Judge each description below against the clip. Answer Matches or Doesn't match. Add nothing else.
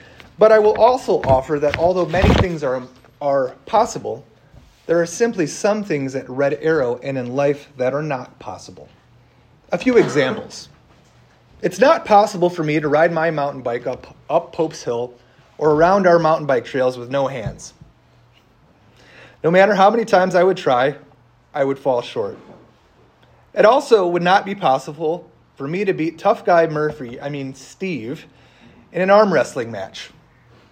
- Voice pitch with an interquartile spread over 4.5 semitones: Matches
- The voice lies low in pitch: Doesn't match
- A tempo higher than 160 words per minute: Matches